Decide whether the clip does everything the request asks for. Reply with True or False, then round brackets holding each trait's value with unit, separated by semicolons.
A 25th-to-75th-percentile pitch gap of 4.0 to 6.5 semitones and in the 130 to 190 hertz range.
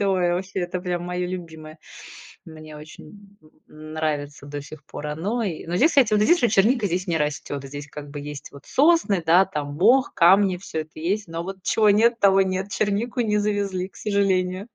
True (4.5 semitones; 185 Hz)